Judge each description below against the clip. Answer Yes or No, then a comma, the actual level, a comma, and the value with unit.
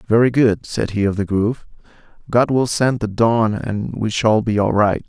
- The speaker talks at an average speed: No, fast, 215 wpm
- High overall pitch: No, low, 110 Hz